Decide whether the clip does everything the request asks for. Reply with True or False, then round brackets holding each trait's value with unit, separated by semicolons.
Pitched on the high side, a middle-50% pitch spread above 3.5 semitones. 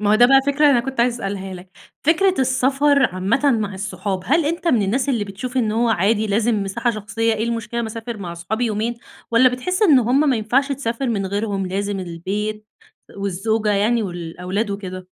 True (220 Hz; 4.0 semitones)